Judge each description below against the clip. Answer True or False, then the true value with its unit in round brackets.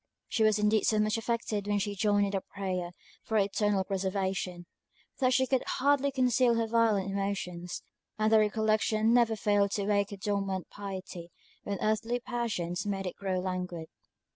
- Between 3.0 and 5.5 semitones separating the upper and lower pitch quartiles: False (2.4 semitones)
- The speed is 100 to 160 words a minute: False (170 wpm)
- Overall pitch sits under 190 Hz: False (205 Hz)